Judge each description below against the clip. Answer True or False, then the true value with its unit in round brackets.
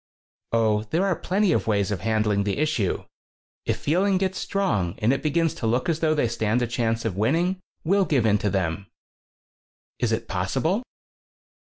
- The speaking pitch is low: True (120 Hz)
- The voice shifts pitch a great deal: True (7.8 semitones)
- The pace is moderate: True (180 wpm)